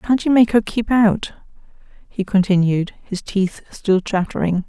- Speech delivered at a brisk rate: No, average, 155 wpm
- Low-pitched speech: No, high, 205 Hz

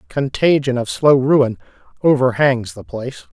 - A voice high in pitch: No, low, 135 Hz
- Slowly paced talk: Yes, slow, 125 wpm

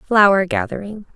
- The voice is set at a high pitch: Yes, high, 205 Hz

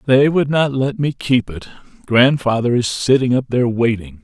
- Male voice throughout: Yes, male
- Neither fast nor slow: Yes, average, 185 wpm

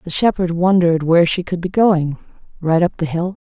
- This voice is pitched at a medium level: Yes, medium, 175 Hz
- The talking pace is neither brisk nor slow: Yes, average, 190 wpm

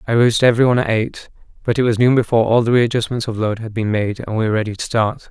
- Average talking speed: No, fast, 270 wpm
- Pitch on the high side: No, low, 115 Hz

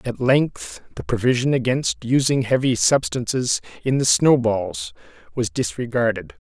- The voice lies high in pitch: No, low, 125 Hz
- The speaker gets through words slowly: Yes, slow, 130 wpm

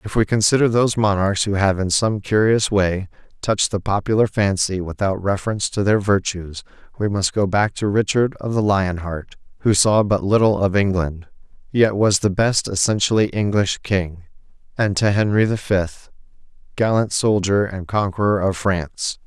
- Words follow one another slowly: No, average, 170 wpm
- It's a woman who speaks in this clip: No, male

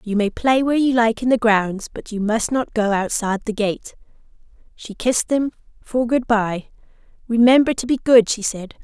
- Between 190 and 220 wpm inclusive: Yes, average, 195 wpm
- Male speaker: No, female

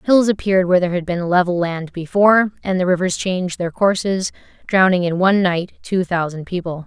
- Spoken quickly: No, average, 190 wpm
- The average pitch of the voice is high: No, medium, 180 Hz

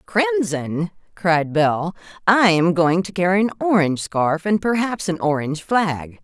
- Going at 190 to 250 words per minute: No, average, 155 wpm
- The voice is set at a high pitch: No, medium, 180 Hz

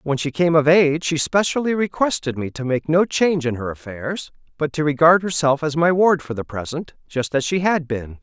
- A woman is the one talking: No, male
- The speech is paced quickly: Yes, fast, 225 wpm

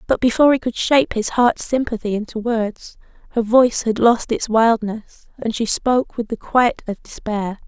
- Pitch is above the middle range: Yes, high, 230 Hz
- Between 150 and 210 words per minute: Yes, average, 190 wpm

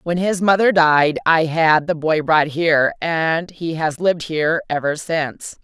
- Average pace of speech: Yes, average, 180 wpm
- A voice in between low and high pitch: Yes, medium, 160 Hz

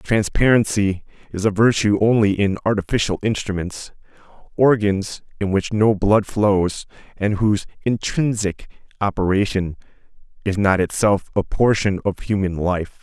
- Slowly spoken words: Yes, slow, 120 wpm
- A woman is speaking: No, male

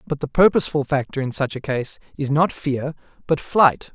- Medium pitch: Yes, medium, 145 Hz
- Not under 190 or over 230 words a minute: Yes, average, 200 wpm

